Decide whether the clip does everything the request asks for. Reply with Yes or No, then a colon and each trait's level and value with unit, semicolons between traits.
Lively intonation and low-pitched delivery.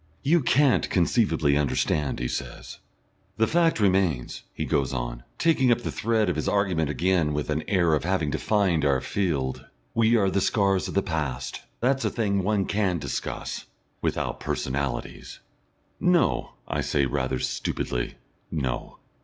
Yes: wide, 6.9 semitones; very low, 90 Hz